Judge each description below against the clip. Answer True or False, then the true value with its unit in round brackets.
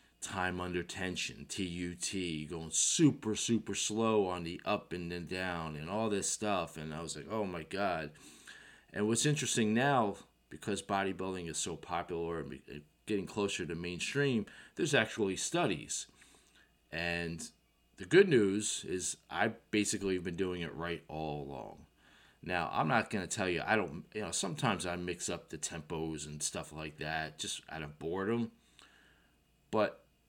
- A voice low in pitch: True (90 Hz)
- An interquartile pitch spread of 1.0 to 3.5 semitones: False (4.1 semitones)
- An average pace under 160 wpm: False (165 wpm)